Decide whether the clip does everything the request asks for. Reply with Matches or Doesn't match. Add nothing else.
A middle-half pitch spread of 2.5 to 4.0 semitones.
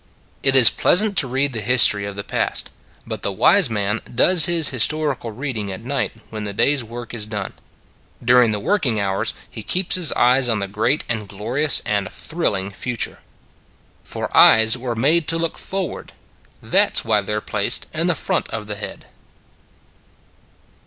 Doesn't match